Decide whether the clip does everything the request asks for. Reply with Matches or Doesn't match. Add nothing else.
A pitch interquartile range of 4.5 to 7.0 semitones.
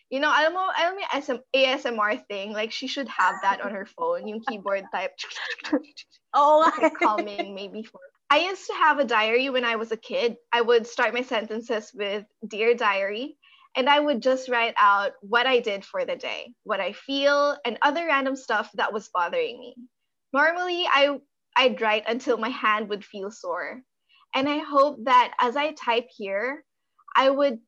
Matches